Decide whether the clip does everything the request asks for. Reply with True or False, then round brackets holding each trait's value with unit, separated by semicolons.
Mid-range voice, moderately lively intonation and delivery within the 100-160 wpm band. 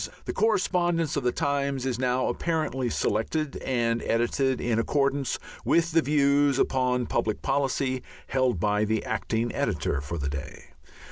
False (130 Hz; 3.6 semitones; 145 wpm)